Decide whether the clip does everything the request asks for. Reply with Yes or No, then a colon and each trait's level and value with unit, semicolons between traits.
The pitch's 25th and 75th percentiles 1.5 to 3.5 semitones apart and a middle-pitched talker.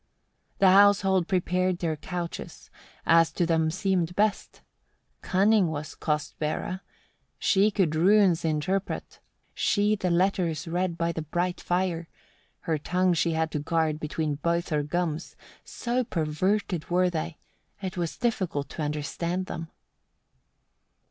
Yes: average, 2.7 semitones; medium, 175 Hz